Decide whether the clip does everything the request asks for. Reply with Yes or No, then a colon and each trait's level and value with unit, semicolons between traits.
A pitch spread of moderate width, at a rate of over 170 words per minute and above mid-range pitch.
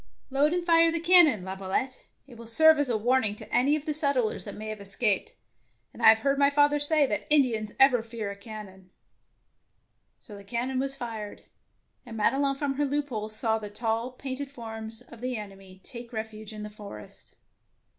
Yes: average, 4.7 semitones; average, 195 wpm; high, 235 Hz